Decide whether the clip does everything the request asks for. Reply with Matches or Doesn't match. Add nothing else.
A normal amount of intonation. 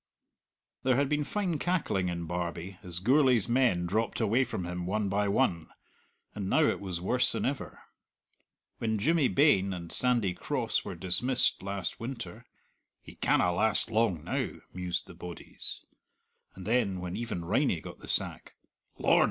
Doesn't match